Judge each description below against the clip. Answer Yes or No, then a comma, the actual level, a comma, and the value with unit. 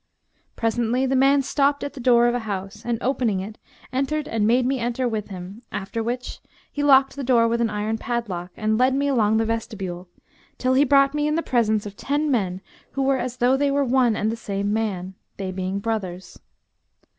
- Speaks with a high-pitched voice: Yes, high, 235 Hz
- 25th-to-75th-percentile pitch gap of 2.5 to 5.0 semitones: Yes, average, 4.1 semitones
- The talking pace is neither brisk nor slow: No, fast, 210 wpm